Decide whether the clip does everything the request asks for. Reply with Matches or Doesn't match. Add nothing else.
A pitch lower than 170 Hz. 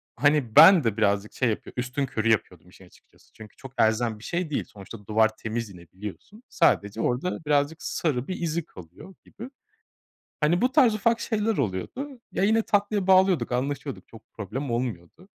Matches